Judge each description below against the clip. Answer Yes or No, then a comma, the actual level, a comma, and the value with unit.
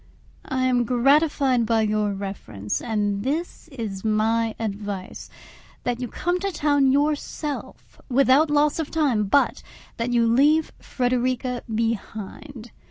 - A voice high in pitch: Yes, high, 245 Hz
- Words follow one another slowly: Yes, slow, 125 wpm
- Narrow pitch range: No, average, 4.8 semitones